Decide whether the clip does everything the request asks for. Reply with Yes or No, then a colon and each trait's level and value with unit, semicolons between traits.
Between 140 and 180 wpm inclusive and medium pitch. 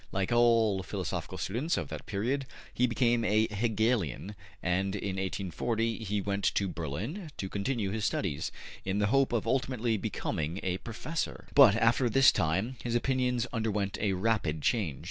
No: average, 160 wpm; low, 110 Hz